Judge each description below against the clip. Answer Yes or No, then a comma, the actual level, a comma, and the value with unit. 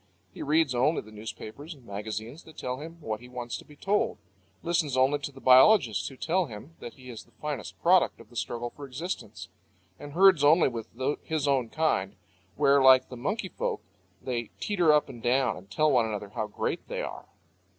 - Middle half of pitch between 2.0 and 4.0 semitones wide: No, average, 4.7 semitones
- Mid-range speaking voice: No, low, 130 Hz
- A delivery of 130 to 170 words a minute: No, average, 200 wpm